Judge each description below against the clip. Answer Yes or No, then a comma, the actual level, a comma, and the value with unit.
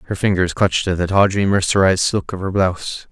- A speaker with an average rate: No, fast, 210 wpm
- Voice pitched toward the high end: No, very low, 95 Hz